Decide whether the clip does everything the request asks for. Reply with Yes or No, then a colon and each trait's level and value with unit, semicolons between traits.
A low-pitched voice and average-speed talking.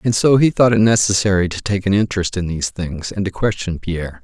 No: low, 100 Hz; fast, 240 wpm